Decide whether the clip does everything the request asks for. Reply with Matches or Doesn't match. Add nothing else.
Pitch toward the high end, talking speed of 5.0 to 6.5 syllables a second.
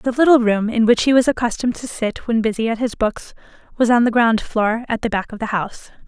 Matches